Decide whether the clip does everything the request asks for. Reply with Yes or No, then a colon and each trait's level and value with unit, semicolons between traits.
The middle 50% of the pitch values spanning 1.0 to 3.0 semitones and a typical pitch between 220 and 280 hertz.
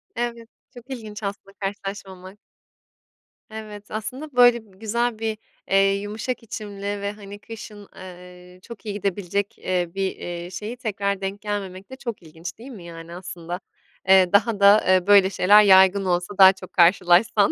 No: narrow, 2.6 semitones; high, 200 Hz